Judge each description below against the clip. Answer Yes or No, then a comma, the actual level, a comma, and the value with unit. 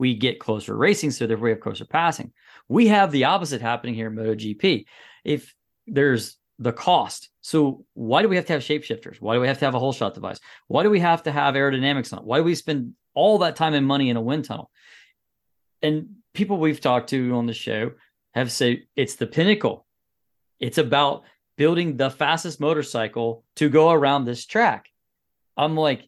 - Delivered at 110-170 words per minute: No, fast, 205 wpm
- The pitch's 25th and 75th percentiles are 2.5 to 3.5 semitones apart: No, average, 4.5 semitones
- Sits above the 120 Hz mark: Yes, medium, 140 Hz